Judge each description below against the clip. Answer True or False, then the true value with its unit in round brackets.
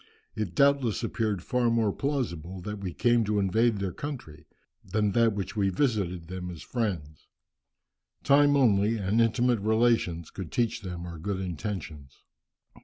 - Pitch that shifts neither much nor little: True (4.6 semitones)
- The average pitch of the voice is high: False (105 Hz)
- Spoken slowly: False (145 wpm)